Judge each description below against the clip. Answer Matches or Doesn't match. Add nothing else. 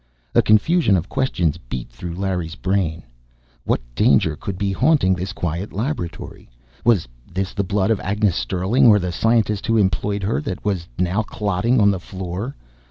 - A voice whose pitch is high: Doesn't match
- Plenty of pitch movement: Doesn't match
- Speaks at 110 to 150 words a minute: Doesn't match